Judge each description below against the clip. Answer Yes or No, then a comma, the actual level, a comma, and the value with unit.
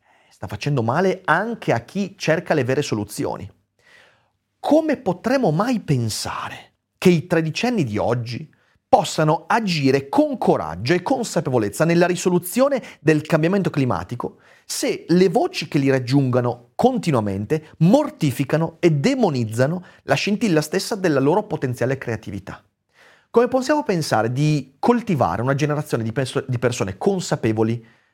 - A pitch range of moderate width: No, wide, 6.9 semitones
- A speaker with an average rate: Yes, average, 125 wpm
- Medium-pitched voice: Yes, medium, 155 Hz